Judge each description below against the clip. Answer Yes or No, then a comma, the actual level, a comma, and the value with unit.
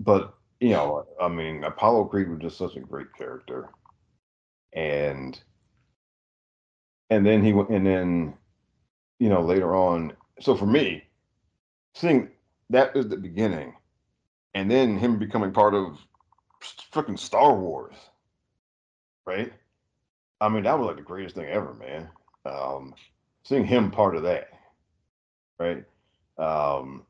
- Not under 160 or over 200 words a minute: No, slow, 135 wpm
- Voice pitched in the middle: No, very low, 90 Hz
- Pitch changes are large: Yes, wide, 6.6 semitones